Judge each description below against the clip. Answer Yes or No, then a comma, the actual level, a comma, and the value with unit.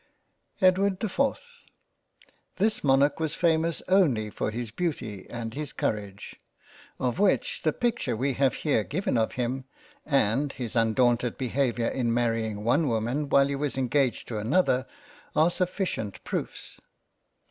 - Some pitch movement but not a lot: No, wide, 5.8 semitones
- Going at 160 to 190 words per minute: No, average, 140 wpm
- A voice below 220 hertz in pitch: Yes, low, 135 Hz